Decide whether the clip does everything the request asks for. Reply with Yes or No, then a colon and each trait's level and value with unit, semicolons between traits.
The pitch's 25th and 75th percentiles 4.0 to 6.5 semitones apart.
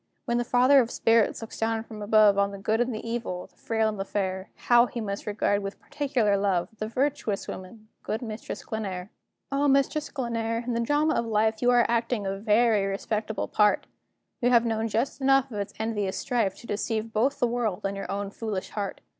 No: average, 2.9 semitones